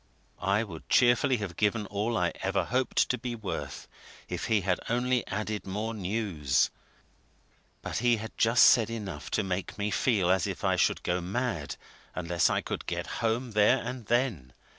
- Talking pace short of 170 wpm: No, average, 175 wpm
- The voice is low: Yes, low, 105 Hz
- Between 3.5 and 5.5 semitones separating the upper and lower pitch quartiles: Yes, average, 4.0 semitones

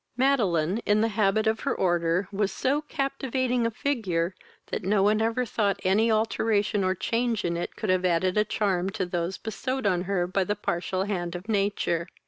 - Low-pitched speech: No, high, 205 Hz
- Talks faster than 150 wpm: Yes, average, 190 wpm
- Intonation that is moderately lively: Yes, average, 3.6 semitones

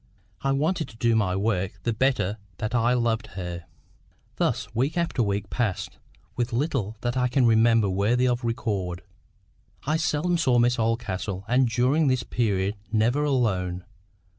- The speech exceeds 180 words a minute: No, average, 155 wpm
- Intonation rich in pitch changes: No, average, 3.9 semitones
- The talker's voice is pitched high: No, low, 115 Hz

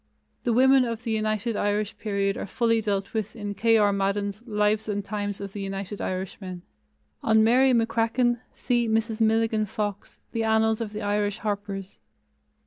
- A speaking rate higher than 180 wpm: No, average, 165 wpm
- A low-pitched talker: No, high, 215 Hz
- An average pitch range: No, narrow, 1.9 semitones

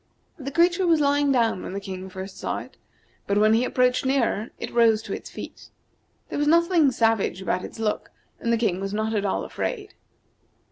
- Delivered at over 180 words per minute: Yes, average, 200 wpm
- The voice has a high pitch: Yes, high, 230 Hz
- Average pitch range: No, wide, 5.9 semitones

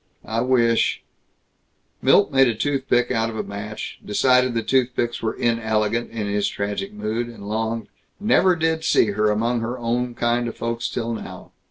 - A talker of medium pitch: No, low, 115 Hz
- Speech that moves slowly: No, average, 175 wpm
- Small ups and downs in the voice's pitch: Yes, narrow, 2.2 semitones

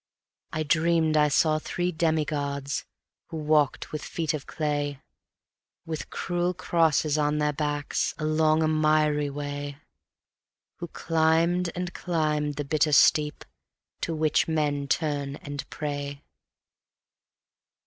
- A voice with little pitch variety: Yes, narrow, 1.6 semitones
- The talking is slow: Yes, slow, 120 wpm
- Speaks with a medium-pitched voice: Yes, medium, 155 Hz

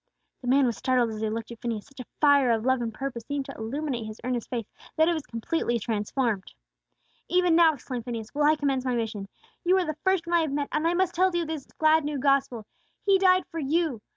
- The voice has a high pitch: Yes, very high, 275 Hz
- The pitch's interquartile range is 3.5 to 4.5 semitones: No, average, 5.3 semitones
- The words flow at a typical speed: No, fast, 245 wpm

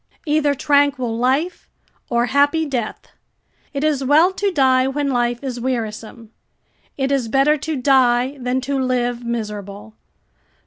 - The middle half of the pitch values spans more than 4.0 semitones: No, average, 3.0 semitones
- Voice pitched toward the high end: Yes, very high, 260 Hz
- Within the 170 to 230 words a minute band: No, slow, 135 wpm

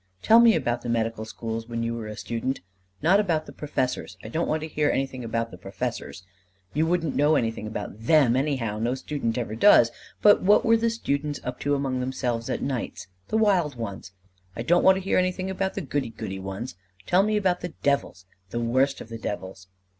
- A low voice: Yes, low, 130 Hz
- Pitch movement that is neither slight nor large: No, wide, 6.3 semitones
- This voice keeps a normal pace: No, fast, 210 wpm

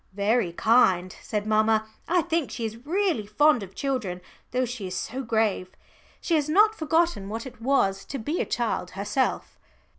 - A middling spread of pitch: No, wide, 6.3 semitones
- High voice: Yes, high, 230 Hz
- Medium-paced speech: Yes, average, 175 wpm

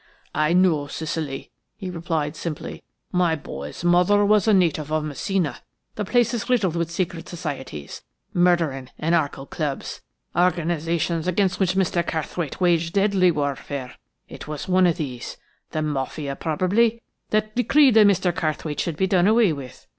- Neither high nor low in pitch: Yes, medium, 170 Hz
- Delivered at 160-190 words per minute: No, average, 145 wpm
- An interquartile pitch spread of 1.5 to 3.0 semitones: No, average, 3.7 semitones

